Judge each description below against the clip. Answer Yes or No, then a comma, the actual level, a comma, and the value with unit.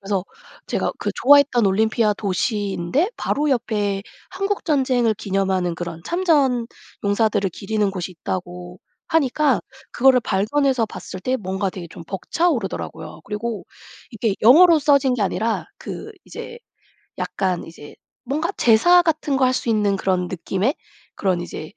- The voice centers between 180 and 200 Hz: No, high, 220 Hz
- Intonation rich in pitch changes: Yes, wide, 6.0 semitones